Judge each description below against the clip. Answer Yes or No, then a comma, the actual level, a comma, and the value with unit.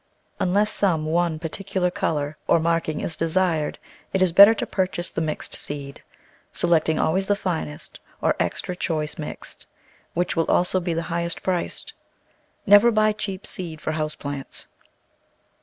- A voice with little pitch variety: No, average, 3.1 semitones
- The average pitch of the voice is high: No, medium, 170 Hz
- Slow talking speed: No, average, 155 wpm